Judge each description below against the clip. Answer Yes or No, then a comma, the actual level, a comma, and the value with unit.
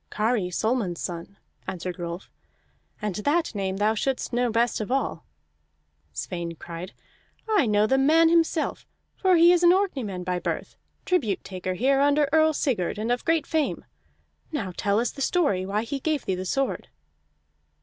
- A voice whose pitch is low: No, high, 230 Hz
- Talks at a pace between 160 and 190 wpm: Yes, average, 165 wpm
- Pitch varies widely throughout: Yes, wide, 7.9 semitones